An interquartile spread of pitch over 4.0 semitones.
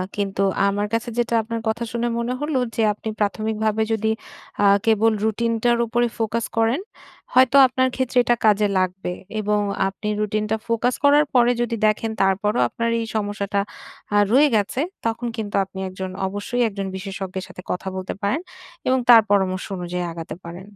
No: average, 2.9 semitones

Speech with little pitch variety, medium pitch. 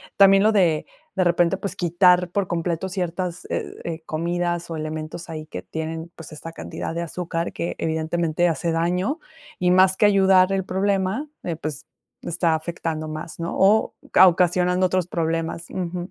Yes: narrow, 2.1 semitones; medium, 175 Hz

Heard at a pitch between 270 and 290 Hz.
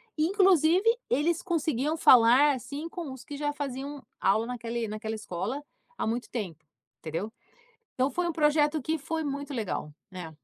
Yes: very high, 280 Hz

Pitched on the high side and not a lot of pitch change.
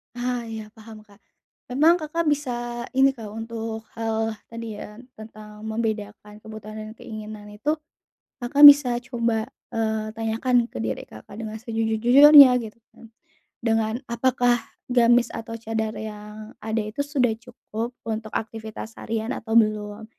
Yes: high, 225 Hz; narrow, 1.9 semitones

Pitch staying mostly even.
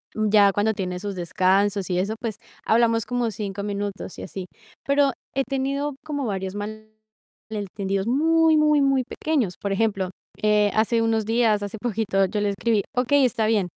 No: average, 3.6 semitones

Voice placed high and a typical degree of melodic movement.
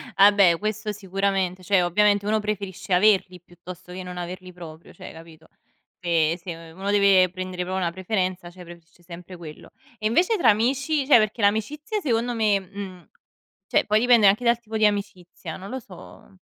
Yes: high, 195 Hz; average, 3.1 semitones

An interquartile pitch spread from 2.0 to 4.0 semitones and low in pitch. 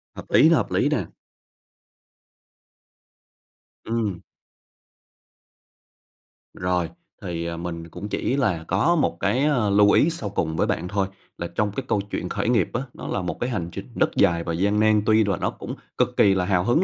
No: average, 4.5 semitones; low, 100 Hz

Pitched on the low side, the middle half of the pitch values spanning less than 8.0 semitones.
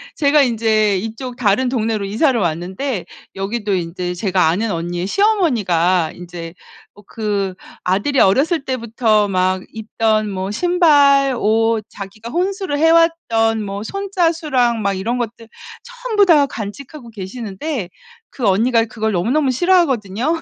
No: high, 225 Hz; wide, 6.2 semitones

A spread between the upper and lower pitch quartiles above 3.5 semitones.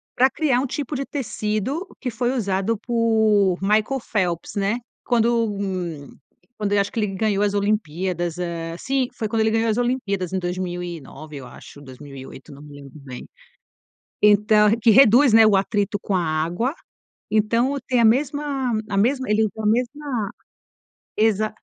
Yes: average, 4.2 semitones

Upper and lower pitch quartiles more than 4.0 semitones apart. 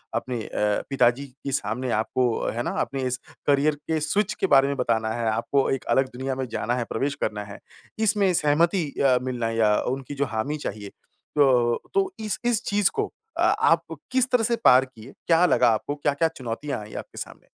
Yes: average, 4.5 semitones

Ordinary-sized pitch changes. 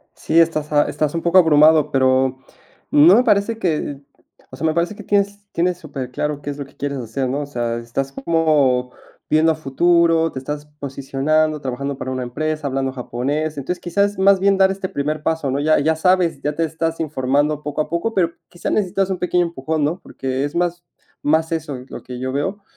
Yes: average, 3.6 semitones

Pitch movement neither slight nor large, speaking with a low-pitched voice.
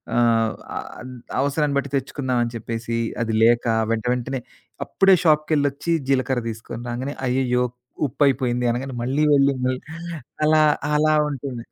Yes: average, 3.1 semitones; low, 130 Hz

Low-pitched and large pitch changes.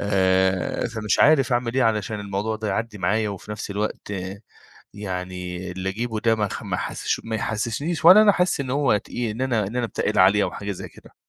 No: low, 105 Hz; average, 3.2 semitones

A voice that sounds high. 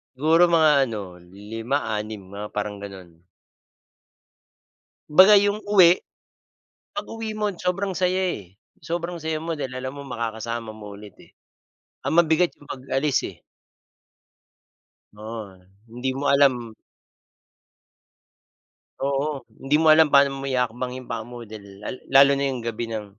No: low, 135 Hz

